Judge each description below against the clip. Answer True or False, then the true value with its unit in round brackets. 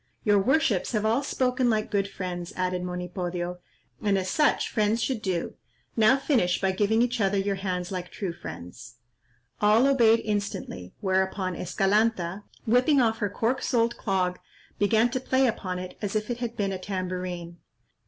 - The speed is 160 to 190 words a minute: True (165 wpm)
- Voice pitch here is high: True (200 Hz)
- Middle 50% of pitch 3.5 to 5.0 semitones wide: True (3.9 semitones)